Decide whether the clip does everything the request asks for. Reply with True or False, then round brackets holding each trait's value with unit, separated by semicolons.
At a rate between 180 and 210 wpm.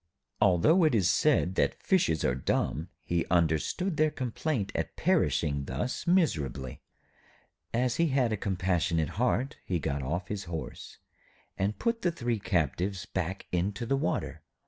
False (145 wpm)